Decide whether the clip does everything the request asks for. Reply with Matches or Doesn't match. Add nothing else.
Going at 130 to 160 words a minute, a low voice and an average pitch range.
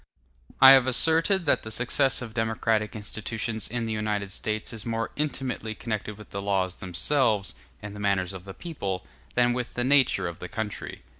Doesn't match